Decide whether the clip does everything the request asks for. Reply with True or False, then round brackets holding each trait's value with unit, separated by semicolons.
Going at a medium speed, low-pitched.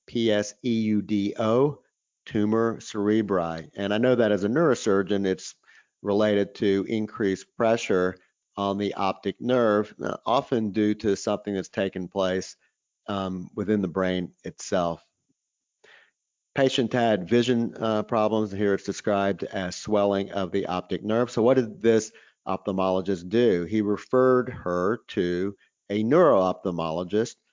False (125 wpm; 105 Hz)